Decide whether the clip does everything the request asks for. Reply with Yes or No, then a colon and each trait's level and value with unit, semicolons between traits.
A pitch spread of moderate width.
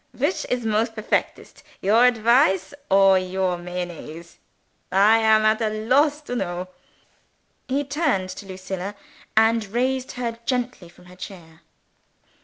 Yes: average, 4.8 semitones